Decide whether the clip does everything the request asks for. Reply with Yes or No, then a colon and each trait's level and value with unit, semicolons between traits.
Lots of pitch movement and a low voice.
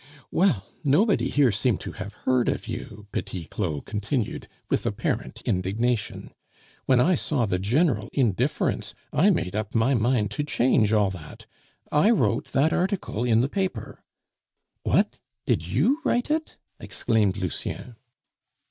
Yes: wide, 6.0 semitones; low, 115 Hz